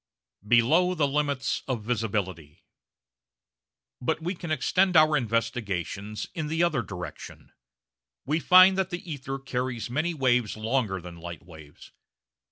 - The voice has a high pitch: No, low, 125 Hz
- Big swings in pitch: Yes, wide, 7.0 semitones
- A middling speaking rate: No, slow, 130 wpm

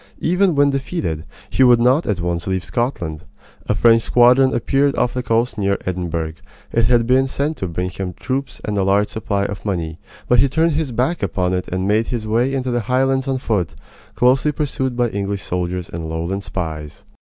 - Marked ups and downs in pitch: Yes, wide, 6.2 semitones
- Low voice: Yes, low, 115 Hz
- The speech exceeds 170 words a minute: Yes, average, 195 wpm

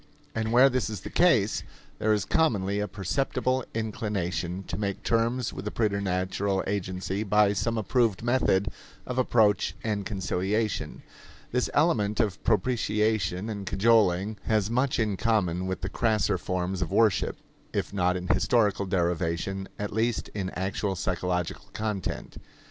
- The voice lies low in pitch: Yes, low, 105 Hz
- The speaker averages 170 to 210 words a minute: No, average, 145 wpm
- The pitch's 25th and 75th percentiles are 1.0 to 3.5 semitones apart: Yes, average, 2.9 semitones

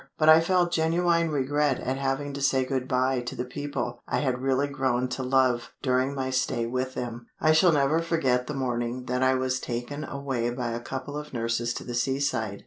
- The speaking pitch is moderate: No, low, 130 Hz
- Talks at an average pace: No, fast, 210 wpm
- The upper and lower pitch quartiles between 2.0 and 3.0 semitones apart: Yes, narrow, 2.6 semitones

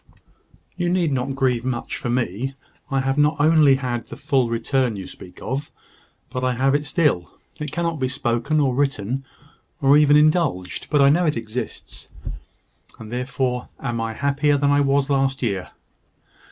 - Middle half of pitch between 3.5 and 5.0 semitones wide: No, average, 3.1 semitones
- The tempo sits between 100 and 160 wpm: No, average, 170 wpm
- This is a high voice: No, low, 135 Hz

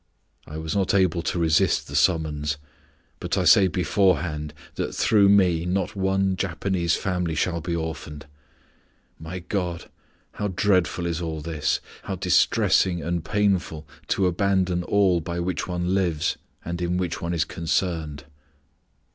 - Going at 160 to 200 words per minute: No, average, 145 wpm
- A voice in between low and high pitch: No, very low, 85 Hz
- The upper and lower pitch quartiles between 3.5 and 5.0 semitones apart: No, narrow, 2.6 semitones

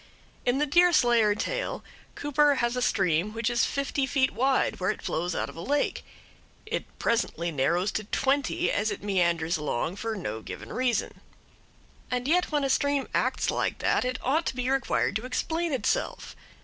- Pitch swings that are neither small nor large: No, wide, 6.2 semitones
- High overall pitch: Yes, high, 245 Hz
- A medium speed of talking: Yes, average, 175 wpm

